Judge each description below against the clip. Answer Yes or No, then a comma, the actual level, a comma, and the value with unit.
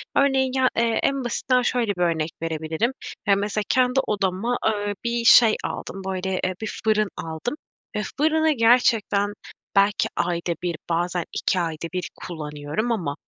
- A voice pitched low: No, high, 205 Hz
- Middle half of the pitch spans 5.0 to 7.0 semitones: Yes, wide, 5.5 semitones